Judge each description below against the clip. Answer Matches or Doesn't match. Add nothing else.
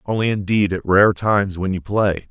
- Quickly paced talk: Matches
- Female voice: Doesn't match